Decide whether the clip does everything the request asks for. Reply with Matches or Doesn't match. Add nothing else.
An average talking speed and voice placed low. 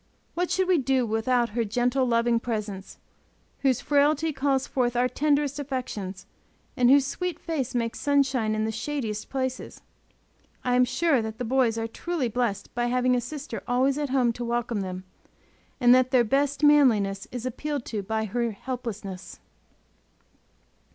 Doesn't match